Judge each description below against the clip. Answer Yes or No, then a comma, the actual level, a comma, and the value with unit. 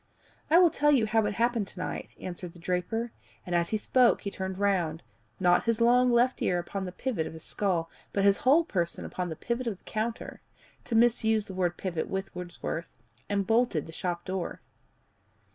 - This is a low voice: No, high, 200 Hz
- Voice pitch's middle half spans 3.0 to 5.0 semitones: Yes, average, 4.7 semitones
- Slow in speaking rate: No, average, 200 wpm